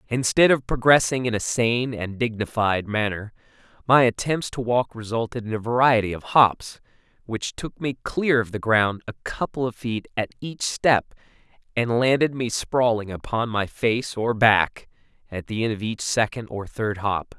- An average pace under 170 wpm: No, average, 175 wpm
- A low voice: Yes, low, 115 Hz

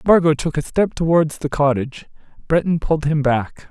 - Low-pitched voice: No, medium, 155 Hz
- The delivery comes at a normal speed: Yes, average, 180 wpm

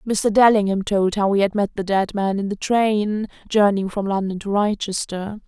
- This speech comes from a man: No, female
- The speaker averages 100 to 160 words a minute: No, average, 195 wpm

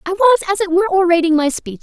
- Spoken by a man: No, female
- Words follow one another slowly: No, fast, 265 wpm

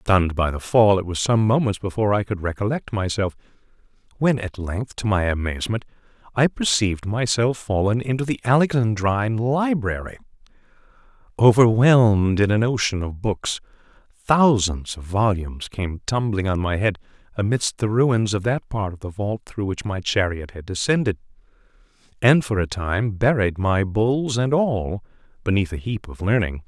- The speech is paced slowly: No, average, 155 wpm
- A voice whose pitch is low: Yes, low, 105 Hz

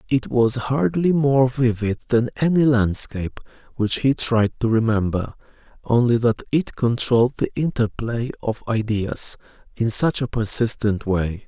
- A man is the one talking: Yes, male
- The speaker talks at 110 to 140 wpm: Yes, slow, 135 wpm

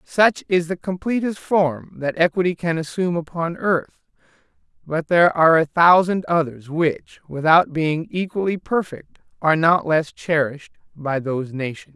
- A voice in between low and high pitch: Yes, medium, 165 Hz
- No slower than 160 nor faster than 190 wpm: No, average, 145 wpm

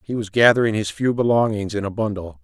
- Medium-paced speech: No, fast, 220 wpm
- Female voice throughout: No, male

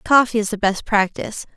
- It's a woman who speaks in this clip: Yes, female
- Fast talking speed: No, average, 190 wpm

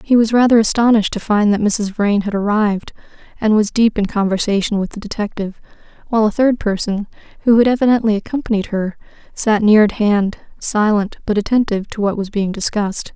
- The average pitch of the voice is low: No, high, 210 Hz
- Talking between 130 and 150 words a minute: No, average, 180 wpm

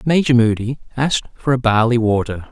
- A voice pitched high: No, low, 120 Hz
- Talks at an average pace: Yes, average, 145 wpm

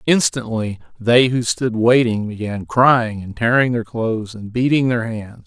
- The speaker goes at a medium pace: Yes, average, 165 wpm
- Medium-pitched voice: No, low, 115 Hz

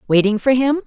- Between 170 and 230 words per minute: Yes, fast, 210 wpm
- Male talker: No, female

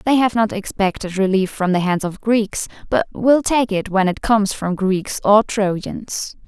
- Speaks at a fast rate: No, average, 195 wpm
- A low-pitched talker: No, high, 205 Hz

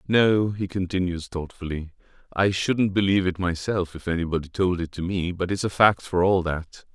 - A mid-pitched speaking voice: No, very low, 90 Hz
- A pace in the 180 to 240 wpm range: Yes, average, 190 wpm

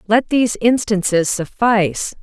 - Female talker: Yes, female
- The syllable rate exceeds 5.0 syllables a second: No, 4.5 syllables/s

